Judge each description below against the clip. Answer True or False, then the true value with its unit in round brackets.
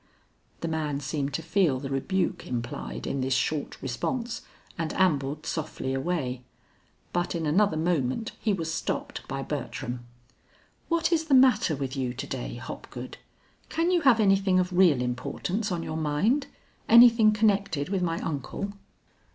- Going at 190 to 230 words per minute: False (150 wpm)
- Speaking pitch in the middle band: True (165 Hz)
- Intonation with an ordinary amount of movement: False (6.7 semitones)